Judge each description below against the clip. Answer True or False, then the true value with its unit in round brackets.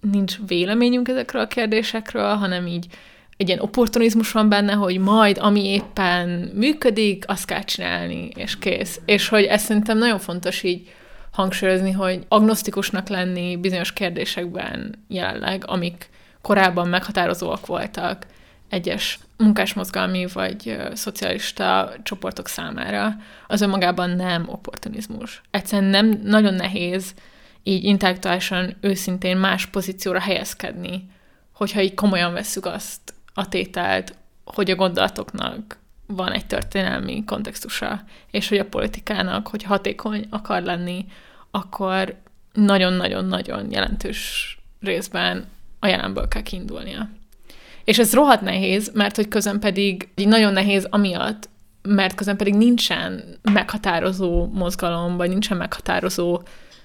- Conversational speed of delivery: True (115 wpm)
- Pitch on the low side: False (195 Hz)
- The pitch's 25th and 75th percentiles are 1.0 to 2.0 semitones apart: False (2.4 semitones)